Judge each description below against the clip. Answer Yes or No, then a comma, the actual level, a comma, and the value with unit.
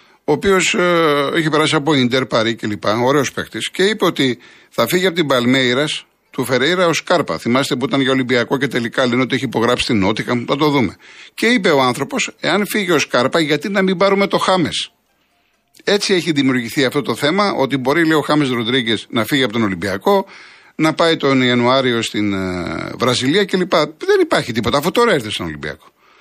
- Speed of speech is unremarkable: No, fast, 195 wpm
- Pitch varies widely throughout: Yes, wide, 5.7 semitones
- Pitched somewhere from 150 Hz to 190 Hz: No, low, 135 Hz